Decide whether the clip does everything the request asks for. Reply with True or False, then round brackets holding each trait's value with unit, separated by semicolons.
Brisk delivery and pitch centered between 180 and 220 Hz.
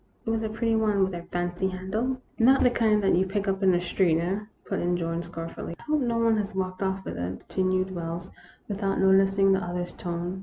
True (260 wpm; 190 Hz)